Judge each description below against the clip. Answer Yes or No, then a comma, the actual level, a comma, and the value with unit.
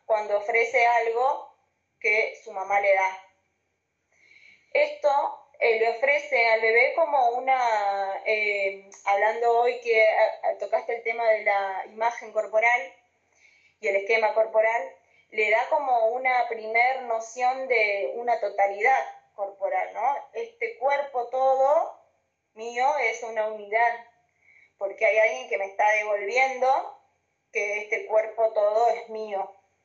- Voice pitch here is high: Yes, high, 230 Hz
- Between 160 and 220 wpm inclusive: No, slow, 125 wpm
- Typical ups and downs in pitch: Yes, average, 3.7 semitones